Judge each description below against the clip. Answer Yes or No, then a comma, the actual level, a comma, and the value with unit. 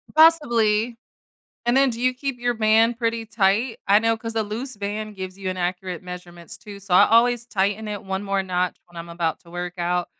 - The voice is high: Yes, high, 210 Hz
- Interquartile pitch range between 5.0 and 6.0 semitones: No, average, 4.0 semitones